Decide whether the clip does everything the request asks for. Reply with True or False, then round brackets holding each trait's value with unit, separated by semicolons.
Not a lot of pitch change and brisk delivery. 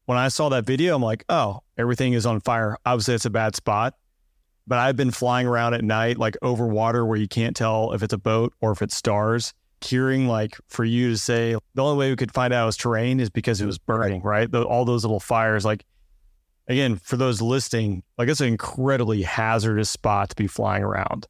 True (2.3 semitones; 230 wpm)